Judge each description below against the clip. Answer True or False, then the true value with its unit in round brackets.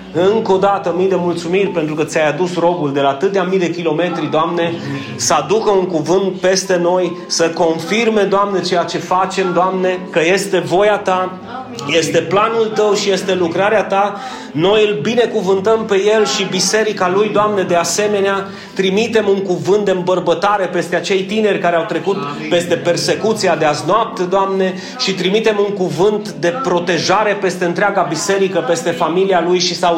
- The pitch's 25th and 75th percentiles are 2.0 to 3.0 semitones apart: True (2.7 semitones)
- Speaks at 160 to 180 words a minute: True (170 wpm)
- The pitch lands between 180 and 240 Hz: True (185 Hz)